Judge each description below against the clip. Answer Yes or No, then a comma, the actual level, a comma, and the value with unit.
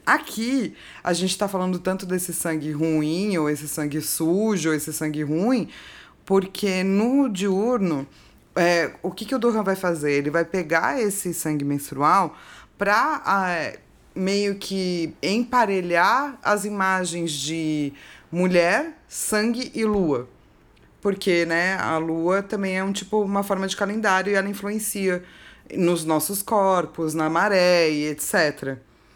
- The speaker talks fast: No, average, 140 wpm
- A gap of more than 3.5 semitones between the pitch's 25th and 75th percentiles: Yes, average, 4.0 semitones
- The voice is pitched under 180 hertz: No, medium, 185 Hz